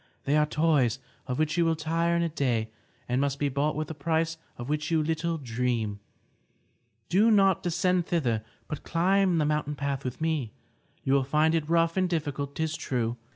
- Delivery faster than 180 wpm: Yes, average, 195 wpm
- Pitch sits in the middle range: Yes, medium, 155 Hz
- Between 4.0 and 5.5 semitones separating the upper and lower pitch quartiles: No, average, 3.3 semitones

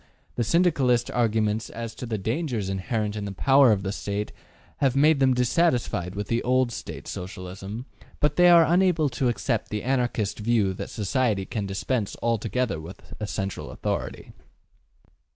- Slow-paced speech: No, average, 160 wpm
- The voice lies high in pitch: No, low, 115 Hz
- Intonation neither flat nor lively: Yes, average, 4.3 semitones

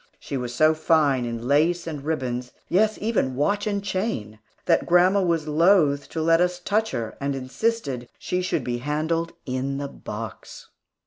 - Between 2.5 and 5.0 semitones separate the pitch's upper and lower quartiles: No, wide, 5.5 semitones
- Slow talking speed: No, average, 170 wpm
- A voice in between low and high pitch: Yes, medium, 155 Hz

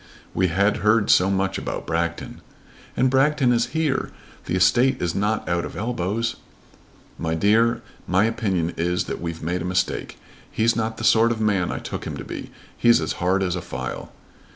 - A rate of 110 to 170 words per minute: No, average, 185 wpm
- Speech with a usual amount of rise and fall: Yes, average, 4.6 semitones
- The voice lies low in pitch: Yes, low, 100 Hz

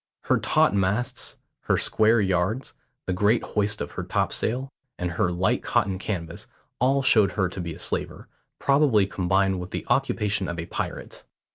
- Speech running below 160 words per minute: No, average, 165 wpm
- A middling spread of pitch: Yes, average, 3.6 semitones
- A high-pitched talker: No, low, 100 Hz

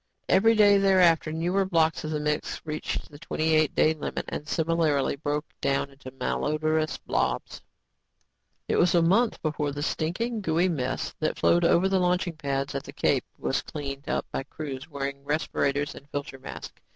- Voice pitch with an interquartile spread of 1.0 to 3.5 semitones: Yes, average, 3.2 semitones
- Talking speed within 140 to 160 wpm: No, average, 175 wpm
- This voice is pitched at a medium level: Yes, medium, 155 Hz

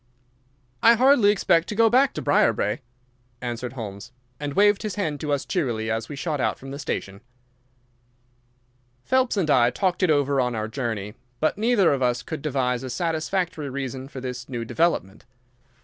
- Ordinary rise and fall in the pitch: No, wide, 6.6 semitones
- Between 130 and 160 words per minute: No, average, 175 wpm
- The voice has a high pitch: No, medium, 140 Hz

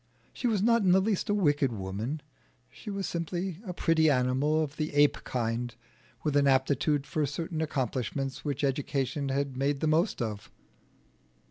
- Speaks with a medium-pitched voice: Yes, medium, 145 Hz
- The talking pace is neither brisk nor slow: Yes, average, 165 wpm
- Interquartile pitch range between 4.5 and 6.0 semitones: No, average, 3.8 semitones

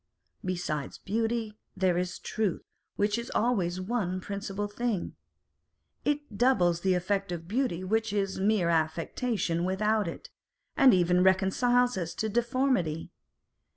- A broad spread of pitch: No, average, 4.1 semitones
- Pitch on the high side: Yes, high, 195 Hz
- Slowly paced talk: Yes, slow, 125 wpm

